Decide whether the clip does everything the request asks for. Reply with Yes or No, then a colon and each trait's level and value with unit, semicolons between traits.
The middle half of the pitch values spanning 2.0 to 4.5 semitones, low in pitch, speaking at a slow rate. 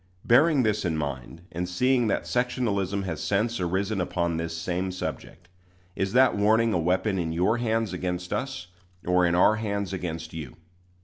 No: average, 4.2 semitones; very low, 95 Hz; average, 170 wpm